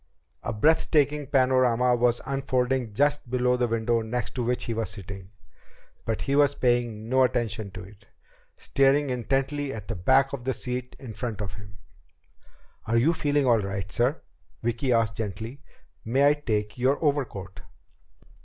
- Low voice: Yes, low, 125 Hz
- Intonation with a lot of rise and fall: No, average, 3.5 semitones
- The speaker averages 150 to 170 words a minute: Yes, average, 165 wpm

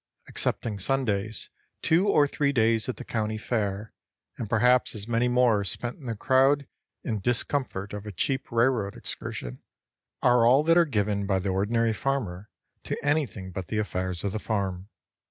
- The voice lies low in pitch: Yes, low, 110 Hz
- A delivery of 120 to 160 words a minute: No, average, 170 wpm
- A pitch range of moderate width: Yes, average, 4.2 semitones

